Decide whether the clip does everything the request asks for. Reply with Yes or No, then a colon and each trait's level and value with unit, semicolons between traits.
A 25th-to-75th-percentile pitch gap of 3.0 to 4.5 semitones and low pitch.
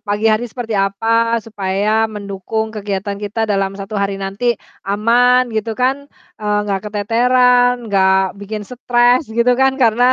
No: average, 3.4 semitones; high, 215 Hz